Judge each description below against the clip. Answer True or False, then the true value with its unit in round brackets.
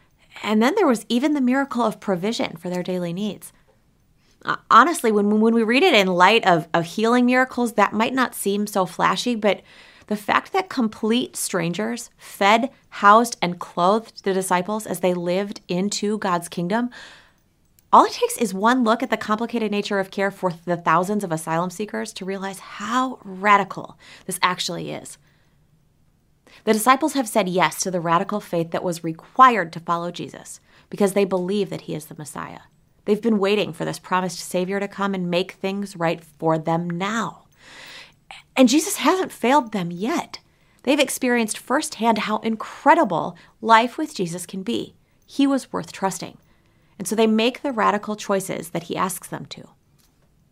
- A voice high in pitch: True (205 Hz)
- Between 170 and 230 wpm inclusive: True (175 wpm)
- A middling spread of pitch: True (4.2 semitones)